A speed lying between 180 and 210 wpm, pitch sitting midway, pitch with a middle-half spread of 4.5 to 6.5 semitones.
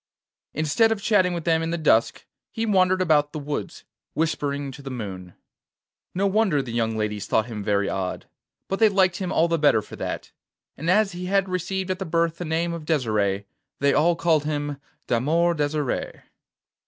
Yes: average, 190 wpm; medium, 160 Hz; average, 5.0 semitones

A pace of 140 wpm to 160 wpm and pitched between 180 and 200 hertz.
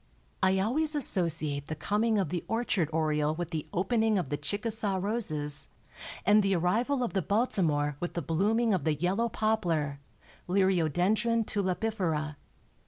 Yes: average, 145 wpm; high, 190 Hz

